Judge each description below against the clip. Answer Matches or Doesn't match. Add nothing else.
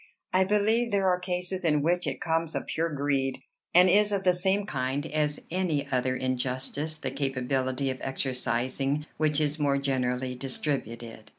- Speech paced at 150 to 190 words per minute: Matches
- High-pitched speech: Doesn't match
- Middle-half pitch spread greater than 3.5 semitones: Matches